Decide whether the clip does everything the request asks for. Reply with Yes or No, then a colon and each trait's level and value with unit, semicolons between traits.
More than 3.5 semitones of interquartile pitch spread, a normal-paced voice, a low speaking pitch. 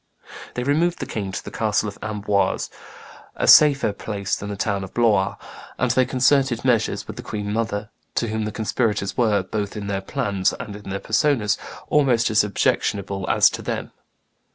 No: average, 3.0 semitones; average, 175 wpm; low, 105 Hz